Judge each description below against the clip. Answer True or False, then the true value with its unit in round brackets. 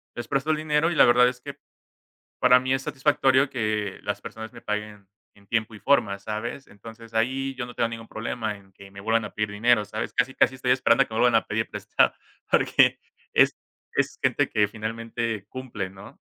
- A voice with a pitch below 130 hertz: True (115 Hz)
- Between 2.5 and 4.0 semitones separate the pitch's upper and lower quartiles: True (3.4 semitones)